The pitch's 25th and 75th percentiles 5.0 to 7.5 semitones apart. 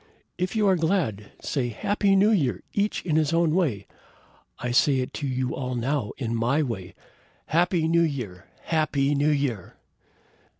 Yes: wide, 5.5 semitones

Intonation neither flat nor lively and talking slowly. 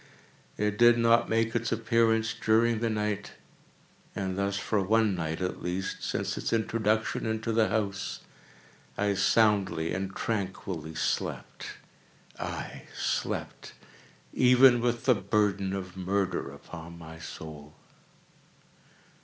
Yes: average, 3.2 semitones; slow, 120 wpm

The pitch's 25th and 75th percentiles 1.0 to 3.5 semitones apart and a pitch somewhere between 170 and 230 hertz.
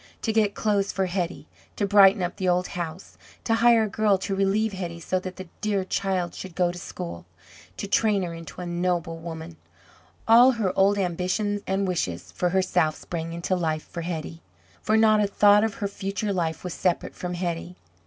Yes: average, 2.8 semitones; medium, 185 Hz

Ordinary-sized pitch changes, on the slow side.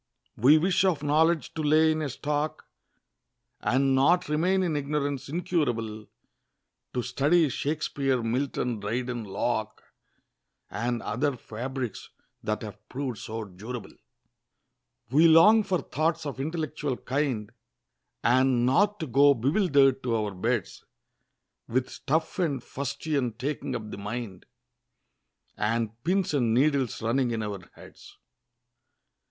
Yes: average, 4.8 semitones; slow, 125 wpm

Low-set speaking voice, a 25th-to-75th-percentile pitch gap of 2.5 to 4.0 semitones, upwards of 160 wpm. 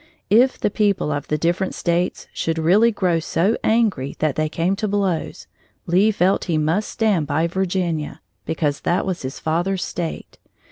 No: medium, 175 Hz; average, 3.7 semitones; average, 170 wpm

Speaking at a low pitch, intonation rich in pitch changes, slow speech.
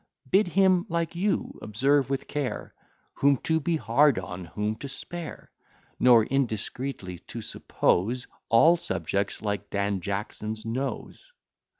Yes: low, 125 Hz; wide, 6.7 semitones; slow, 125 wpm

